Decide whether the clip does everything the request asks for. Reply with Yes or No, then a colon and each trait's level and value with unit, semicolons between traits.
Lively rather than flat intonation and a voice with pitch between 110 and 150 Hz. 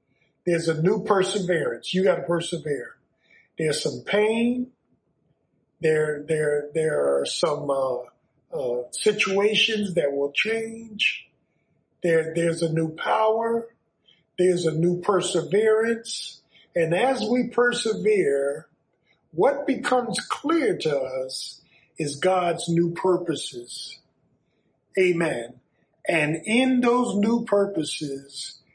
No: wide, 6.0 semitones; medium, 175 Hz